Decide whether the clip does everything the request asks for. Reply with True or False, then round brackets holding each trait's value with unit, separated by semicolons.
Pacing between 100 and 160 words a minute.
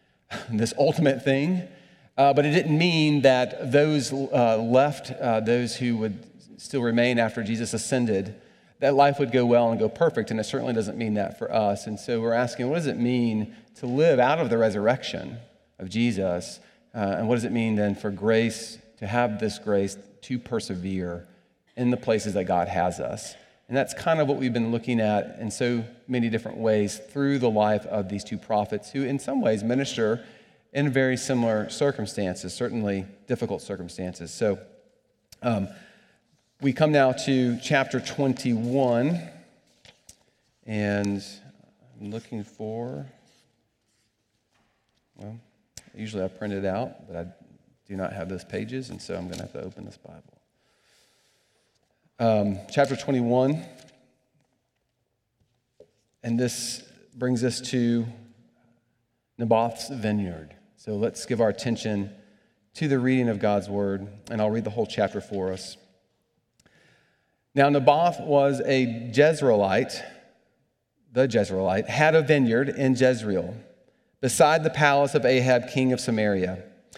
True (150 wpm)